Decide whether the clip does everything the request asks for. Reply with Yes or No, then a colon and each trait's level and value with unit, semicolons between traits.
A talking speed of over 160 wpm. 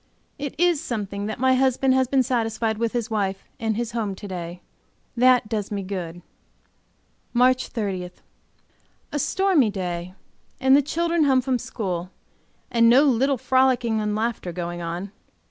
No: average, 155 wpm